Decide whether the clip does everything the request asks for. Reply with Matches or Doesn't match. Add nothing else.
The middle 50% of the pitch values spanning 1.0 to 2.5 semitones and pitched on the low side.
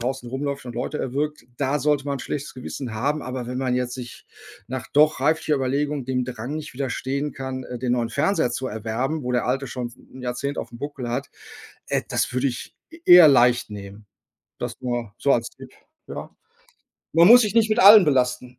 Doesn't match